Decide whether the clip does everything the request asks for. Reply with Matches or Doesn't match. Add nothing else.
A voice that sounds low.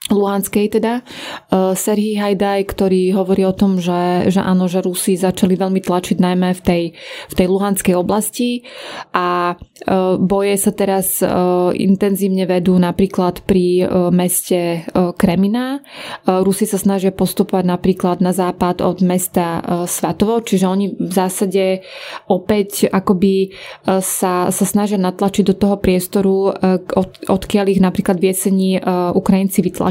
Doesn't match